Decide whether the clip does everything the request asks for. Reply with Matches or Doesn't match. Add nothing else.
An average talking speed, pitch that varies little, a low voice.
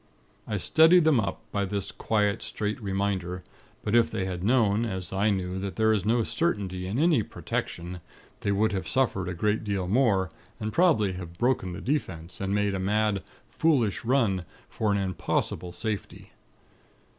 Doesn't match